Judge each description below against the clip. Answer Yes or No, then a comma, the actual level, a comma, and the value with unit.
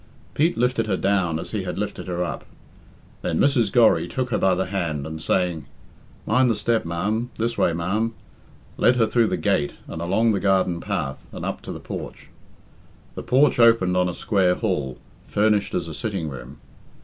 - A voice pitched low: Yes, very low, 95 Hz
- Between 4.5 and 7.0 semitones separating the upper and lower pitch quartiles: Yes, average, 4.9 semitones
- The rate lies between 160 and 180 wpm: No, average, 190 wpm